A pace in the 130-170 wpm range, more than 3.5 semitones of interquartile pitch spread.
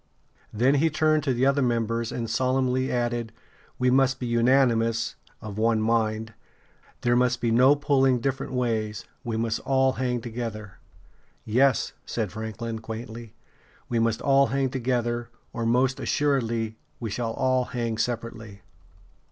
No: average, 145 wpm; narrow, 2.4 semitones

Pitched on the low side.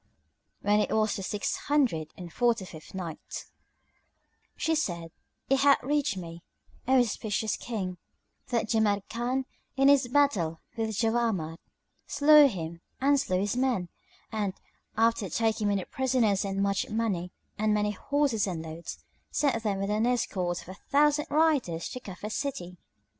No: high, 215 Hz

